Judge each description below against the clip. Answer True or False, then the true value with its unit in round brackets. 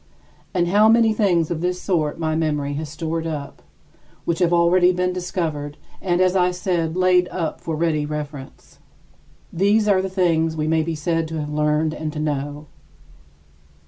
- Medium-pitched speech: True (165 Hz)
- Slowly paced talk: False (175 wpm)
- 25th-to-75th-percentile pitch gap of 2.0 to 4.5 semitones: True (2.9 semitones)